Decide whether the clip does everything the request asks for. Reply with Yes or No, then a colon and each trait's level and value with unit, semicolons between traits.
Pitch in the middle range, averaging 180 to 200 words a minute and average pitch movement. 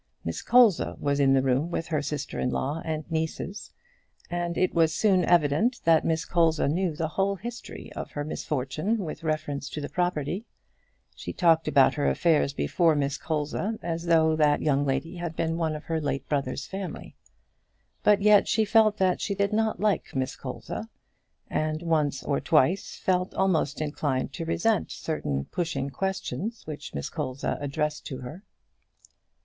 No: medium, 160 Hz; average, 170 wpm; average, 4.0 semitones